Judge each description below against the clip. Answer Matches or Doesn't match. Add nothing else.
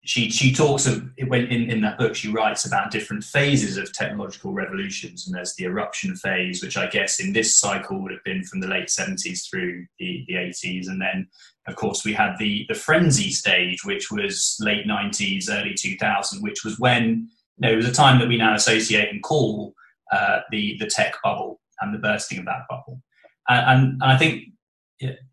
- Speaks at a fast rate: Matches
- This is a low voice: Matches